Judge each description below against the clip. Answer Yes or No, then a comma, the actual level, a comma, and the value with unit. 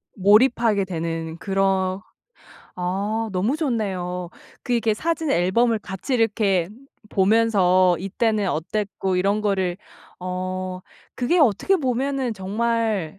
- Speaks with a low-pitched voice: No, high, 200 Hz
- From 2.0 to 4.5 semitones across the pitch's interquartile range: Yes, average, 3.8 semitones